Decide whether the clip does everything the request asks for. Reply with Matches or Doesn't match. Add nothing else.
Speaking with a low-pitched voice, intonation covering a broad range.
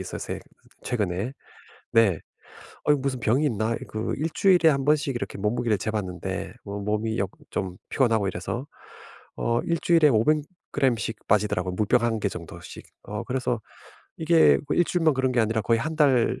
Doesn't match